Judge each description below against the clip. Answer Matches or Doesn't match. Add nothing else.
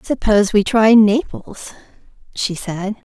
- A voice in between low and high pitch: Doesn't match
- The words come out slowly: Matches